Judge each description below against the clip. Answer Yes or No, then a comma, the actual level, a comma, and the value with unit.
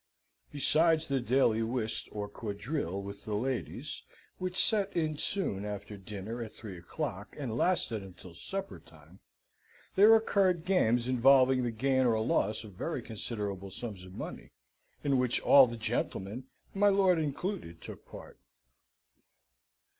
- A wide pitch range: Yes, wide, 7.0 semitones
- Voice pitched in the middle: No, low, 120 Hz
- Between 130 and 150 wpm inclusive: Yes, average, 140 wpm